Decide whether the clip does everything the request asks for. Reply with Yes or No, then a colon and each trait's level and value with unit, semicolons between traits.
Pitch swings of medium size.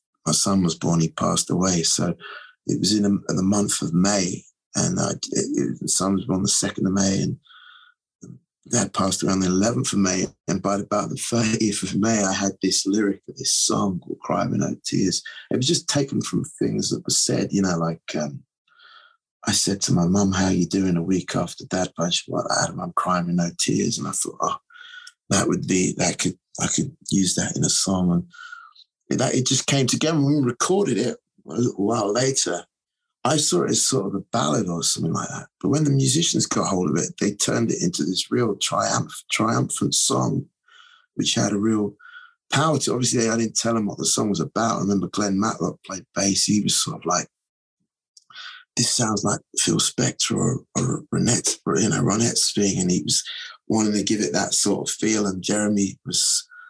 No: wide, 7.1 semitones